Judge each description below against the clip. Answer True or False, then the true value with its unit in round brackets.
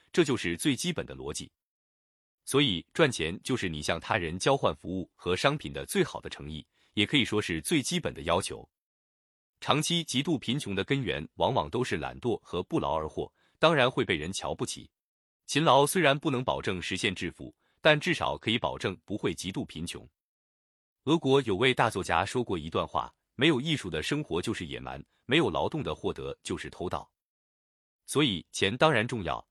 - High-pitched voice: False (115 Hz)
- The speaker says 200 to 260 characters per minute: False (280 characters per minute)